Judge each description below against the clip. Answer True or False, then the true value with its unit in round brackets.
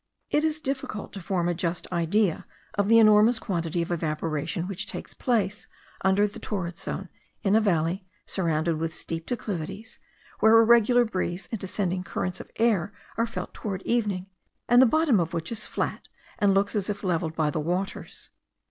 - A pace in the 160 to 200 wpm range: True (180 wpm)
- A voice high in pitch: True (195 Hz)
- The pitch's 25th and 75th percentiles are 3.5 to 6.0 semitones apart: True (4.4 semitones)